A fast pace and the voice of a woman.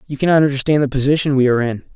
No: fast, 245 wpm; male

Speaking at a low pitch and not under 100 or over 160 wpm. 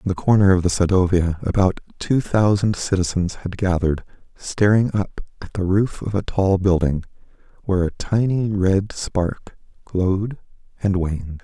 Yes: very low, 95 Hz; average, 150 wpm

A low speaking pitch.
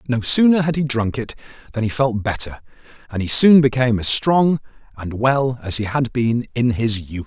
Yes: low, 120 Hz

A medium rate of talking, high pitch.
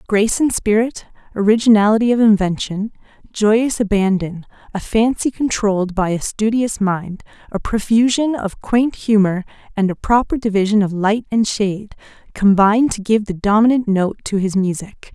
Yes: average, 145 wpm; high, 210 Hz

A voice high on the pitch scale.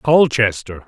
No: low, 120 Hz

